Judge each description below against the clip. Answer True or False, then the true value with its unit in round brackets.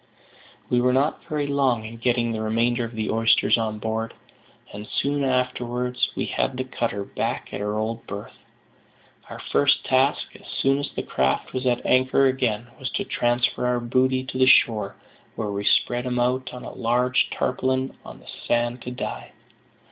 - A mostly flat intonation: True (2.2 semitones)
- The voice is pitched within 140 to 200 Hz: False (125 Hz)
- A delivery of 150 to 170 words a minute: False (180 wpm)